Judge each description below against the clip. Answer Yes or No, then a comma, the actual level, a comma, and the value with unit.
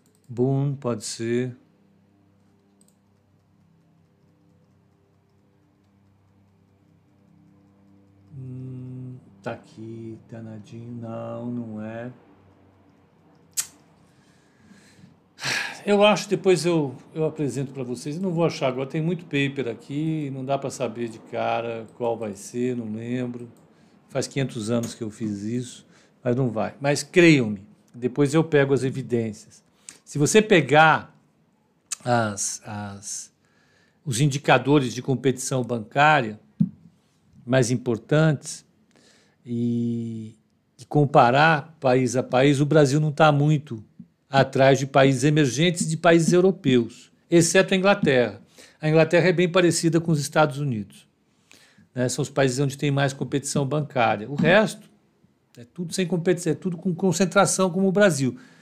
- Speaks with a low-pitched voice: Yes, low, 130 Hz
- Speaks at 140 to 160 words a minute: No, average, 125 wpm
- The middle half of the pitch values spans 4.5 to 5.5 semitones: Yes, average, 5.1 semitones